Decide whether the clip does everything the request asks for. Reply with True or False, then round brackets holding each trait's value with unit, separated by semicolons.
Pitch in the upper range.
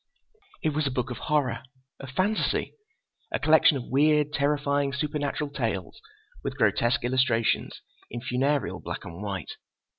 False (140 Hz)